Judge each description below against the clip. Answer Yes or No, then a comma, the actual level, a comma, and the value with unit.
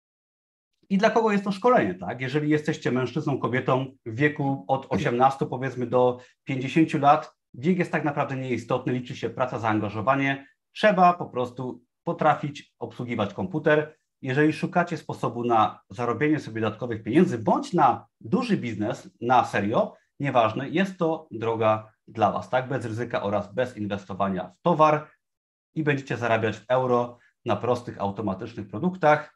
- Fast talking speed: No, average, 145 wpm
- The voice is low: Yes, low, 130 Hz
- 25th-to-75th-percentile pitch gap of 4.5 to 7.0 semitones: Yes, average, 4.9 semitones